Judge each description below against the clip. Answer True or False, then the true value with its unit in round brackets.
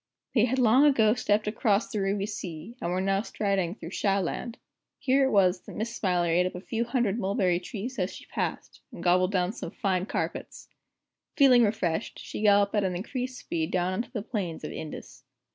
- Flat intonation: False (4.1 semitones)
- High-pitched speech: True (200 Hz)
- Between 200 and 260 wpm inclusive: True (205 wpm)